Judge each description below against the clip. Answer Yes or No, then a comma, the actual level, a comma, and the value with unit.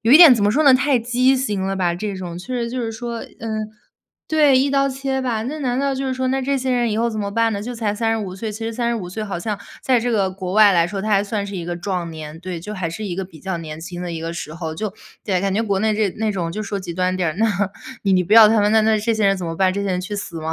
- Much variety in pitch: No, average, 4.2 semitones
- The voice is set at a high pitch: Yes, high, 210 Hz